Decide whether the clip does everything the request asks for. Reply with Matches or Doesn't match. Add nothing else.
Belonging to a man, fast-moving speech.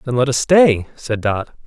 Matches